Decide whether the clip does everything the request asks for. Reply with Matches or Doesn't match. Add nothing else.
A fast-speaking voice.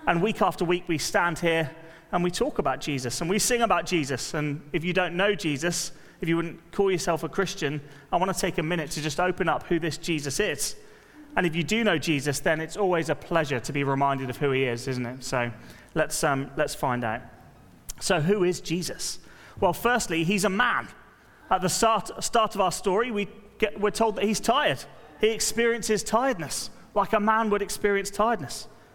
Matches